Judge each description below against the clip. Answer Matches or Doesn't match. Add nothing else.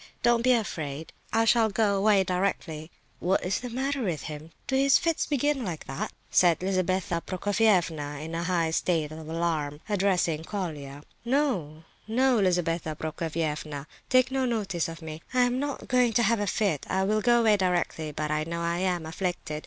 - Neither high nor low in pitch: Matches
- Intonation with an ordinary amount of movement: Doesn't match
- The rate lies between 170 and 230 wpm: Matches